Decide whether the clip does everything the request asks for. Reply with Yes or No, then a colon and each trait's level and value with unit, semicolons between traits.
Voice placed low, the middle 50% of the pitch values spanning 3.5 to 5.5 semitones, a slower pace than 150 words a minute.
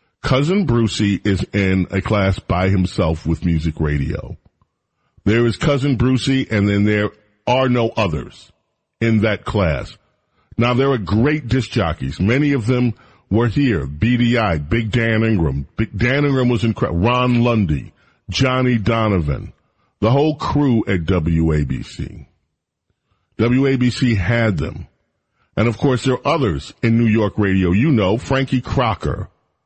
Yes: low, 110 Hz; average, 4.5 semitones; average, 140 wpm